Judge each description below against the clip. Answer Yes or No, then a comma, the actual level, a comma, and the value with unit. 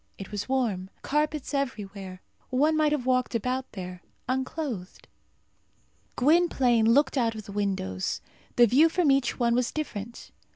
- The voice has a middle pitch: No, very high, 250 Hz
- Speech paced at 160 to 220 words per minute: No, average, 140 wpm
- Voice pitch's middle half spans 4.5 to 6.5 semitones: Yes, average, 5.3 semitones